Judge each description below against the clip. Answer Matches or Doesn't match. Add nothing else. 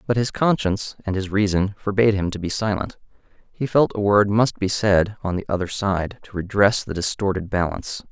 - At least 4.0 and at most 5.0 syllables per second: Doesn't match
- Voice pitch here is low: Matches